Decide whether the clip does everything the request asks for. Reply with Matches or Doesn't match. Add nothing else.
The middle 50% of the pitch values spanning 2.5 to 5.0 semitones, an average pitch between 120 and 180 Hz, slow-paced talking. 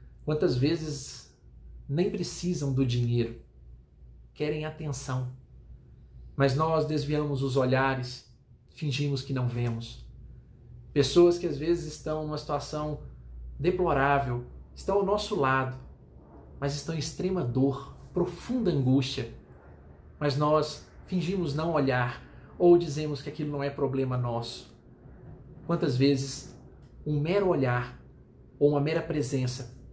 Matches